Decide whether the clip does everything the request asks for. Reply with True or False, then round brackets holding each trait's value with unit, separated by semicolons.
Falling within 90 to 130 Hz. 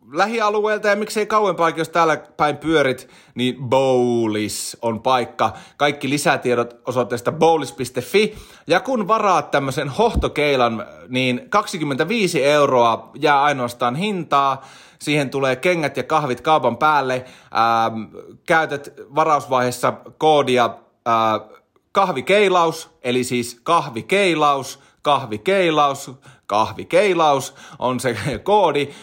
False (140 Hz)